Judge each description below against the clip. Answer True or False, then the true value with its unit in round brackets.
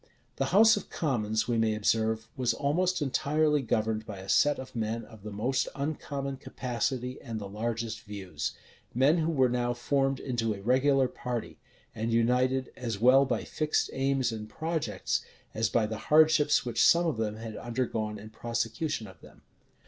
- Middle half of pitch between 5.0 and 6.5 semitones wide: False (3.8 semitones)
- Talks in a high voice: False (120 Hz)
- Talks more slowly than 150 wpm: False (170 wpm)